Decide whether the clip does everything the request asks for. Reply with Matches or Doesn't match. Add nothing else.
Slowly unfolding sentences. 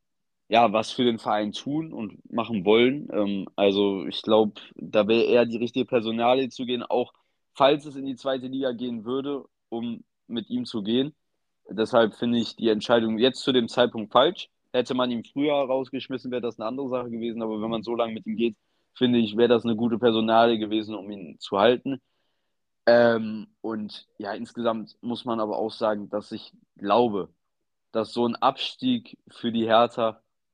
Doesn't match